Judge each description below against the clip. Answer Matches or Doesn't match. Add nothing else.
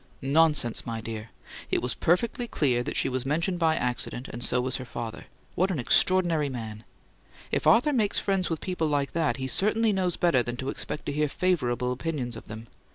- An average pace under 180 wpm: Doesn't match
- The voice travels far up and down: Matches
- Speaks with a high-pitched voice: Doesn't match